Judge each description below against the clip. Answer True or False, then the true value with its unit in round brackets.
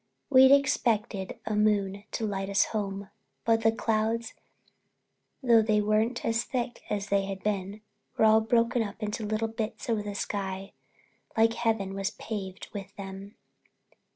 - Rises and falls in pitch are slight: True (2.2 semitones)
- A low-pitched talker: False (215 Hz)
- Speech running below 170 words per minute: True (155 wpm)